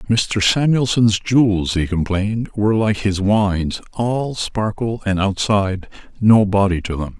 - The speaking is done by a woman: No, male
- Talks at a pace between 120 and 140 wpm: Yes, slow, 135 wpm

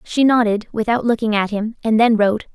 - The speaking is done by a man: No, female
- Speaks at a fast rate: Yes, fast, 210 wpm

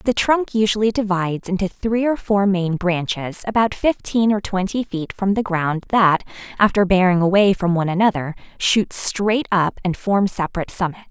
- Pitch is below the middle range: No, high, 195 Hz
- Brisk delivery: No, average, 175 wpm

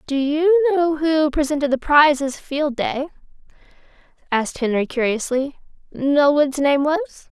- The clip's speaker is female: Yes, female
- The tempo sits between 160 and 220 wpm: No, average, 140 wpm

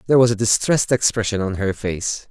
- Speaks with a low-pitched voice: Yes, low, 105 Hz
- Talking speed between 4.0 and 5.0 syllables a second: No, 6.1 syllables/s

